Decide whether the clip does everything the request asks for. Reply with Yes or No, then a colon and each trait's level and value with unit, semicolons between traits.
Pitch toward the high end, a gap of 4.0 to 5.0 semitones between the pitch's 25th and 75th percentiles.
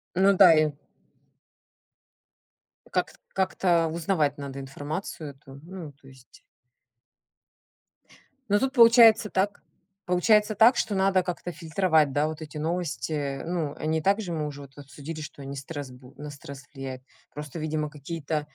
No: medium, 155 Hz; average, 4.5 semitones